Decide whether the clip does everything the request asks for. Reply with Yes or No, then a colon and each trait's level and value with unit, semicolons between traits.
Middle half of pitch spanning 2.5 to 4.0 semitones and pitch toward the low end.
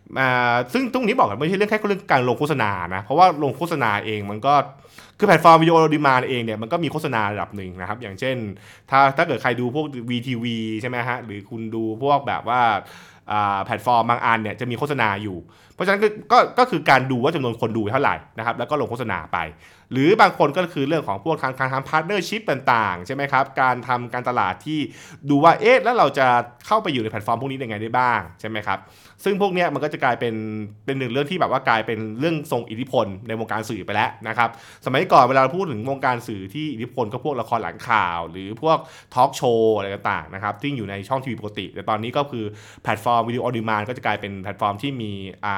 No: wide, 5.4 semitones; low, 125 Hz